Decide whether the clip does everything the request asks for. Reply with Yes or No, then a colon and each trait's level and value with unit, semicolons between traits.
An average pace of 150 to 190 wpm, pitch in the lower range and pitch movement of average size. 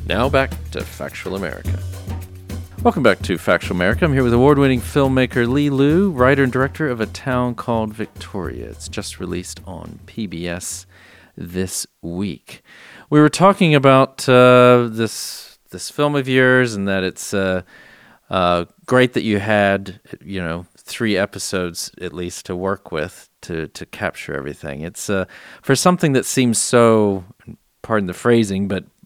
No: average, 155 wpm; low, 105 Hz; wide, 5.8 semitones